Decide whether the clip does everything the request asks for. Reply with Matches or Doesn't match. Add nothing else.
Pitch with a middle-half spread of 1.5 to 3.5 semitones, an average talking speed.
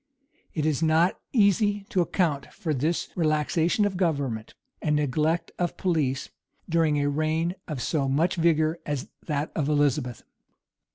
Matches